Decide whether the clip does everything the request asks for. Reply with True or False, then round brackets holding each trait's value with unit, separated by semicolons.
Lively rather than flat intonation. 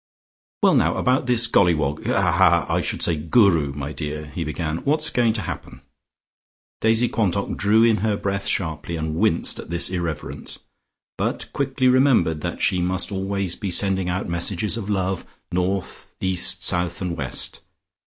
False (4.6 semitones)